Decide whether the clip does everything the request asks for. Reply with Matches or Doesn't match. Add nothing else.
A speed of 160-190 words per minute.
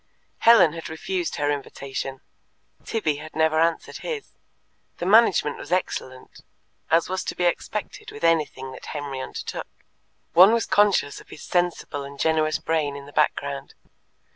Doesn't match